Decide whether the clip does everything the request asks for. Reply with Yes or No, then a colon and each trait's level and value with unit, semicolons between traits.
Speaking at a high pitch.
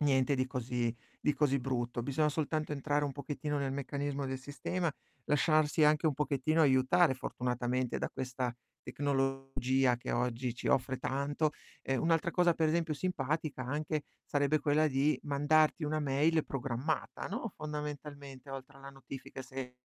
No: medium, 140 Hz